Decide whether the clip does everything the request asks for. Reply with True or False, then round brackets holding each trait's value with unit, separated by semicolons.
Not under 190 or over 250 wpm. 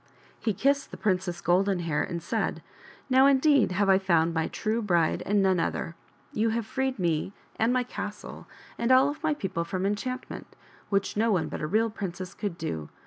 True (200 wpm)